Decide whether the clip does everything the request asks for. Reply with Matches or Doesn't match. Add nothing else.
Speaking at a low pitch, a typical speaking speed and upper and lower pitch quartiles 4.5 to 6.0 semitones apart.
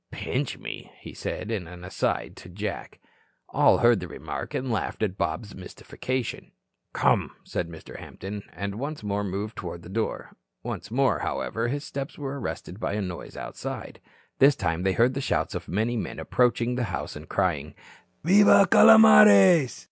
Matches